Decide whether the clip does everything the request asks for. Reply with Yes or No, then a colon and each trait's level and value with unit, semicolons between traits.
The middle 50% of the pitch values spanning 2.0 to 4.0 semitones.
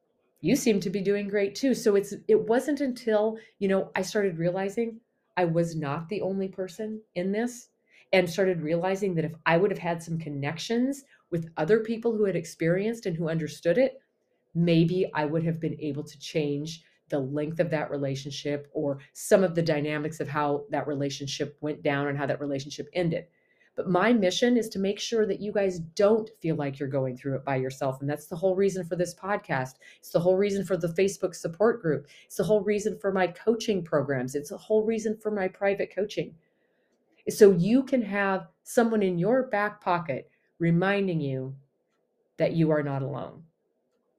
No: wide, 5.4 semitones